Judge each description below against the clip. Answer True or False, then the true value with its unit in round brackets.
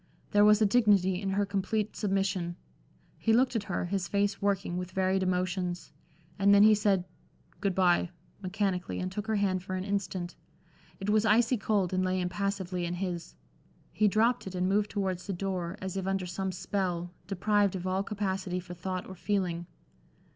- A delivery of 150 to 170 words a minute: False (185 wpm)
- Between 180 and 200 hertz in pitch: True (190 Hz)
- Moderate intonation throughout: False (1.9 semitones)